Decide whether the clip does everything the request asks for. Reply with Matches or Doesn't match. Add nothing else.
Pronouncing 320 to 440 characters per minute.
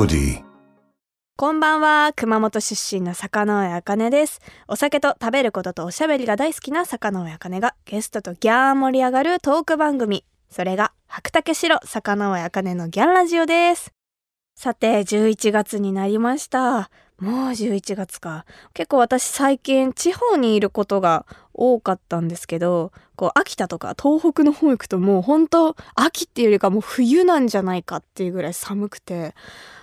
Doesn't match